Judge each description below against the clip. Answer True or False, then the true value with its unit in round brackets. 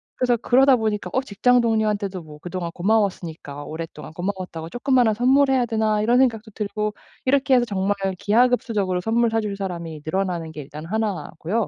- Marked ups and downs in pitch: False (4.9 semitones)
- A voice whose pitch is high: True (210 Hz)